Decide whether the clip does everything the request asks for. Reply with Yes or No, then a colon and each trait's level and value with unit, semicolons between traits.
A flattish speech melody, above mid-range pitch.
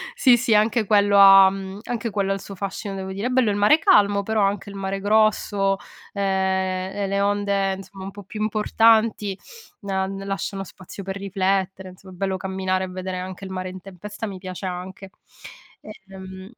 Yes: narrow, 1.3 semitones; high, 195 Hz